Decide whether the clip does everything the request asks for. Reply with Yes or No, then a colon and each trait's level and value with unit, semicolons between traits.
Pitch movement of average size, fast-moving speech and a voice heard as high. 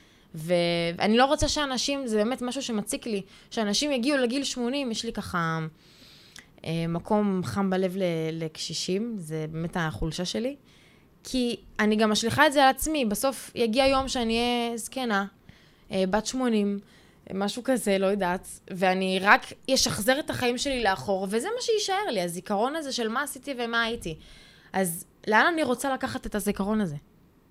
No: wide, 5.8 semitones; fast, 155 wpm; high, 215 Hz